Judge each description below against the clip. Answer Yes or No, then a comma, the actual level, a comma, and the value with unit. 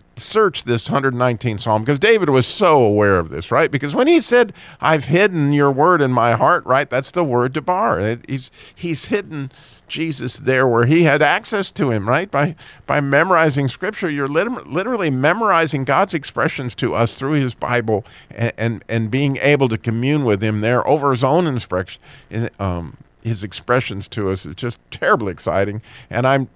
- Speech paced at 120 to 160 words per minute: No, average, 185 wpm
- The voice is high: No, low, 130 Hz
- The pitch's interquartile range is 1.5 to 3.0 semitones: No, average, 4.6 semitones